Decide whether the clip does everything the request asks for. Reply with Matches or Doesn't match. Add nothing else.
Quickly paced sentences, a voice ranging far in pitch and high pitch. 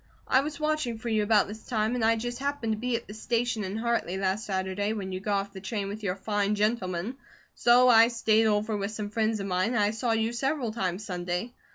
Doesn't match